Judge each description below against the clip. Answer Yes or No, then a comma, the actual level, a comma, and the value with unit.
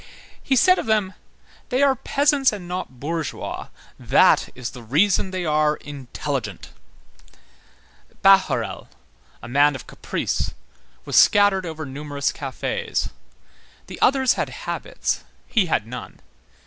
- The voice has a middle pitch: Yes, medium, 180 Hz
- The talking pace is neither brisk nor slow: No, slow, 120 wpm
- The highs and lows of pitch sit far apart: Yes, wide, 7.4 semitones